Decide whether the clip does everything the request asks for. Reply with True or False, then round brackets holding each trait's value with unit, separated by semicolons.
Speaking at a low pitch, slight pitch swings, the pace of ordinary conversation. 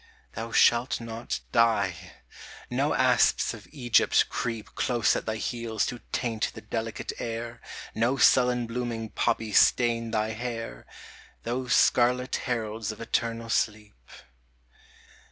False (115 Hz; 1.4 semitones; 120 wpm)